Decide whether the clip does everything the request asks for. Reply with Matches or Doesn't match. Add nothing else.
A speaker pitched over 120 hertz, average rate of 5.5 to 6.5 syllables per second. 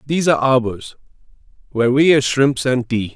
Matches